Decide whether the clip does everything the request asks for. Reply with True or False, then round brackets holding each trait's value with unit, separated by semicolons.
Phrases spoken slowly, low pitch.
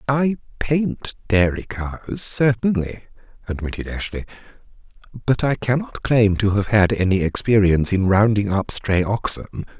True (130 wpm; 110 Hz)